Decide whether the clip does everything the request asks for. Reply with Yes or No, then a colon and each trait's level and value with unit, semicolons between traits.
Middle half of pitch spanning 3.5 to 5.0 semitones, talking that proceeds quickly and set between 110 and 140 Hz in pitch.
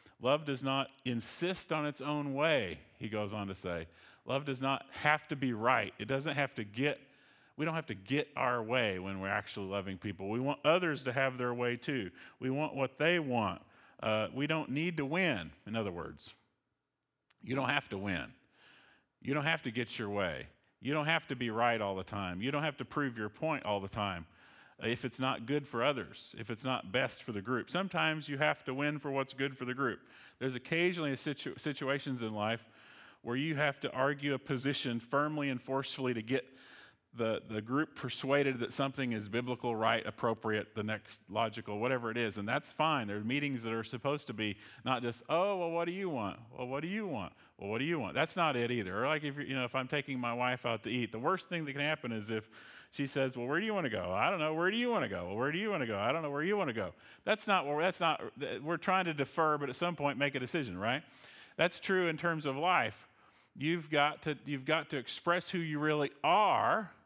Yes: average, 4.6 semitones; fast, 240 wpm; low, 135 Hz